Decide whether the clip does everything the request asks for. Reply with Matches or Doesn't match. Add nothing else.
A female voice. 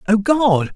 Doesn't match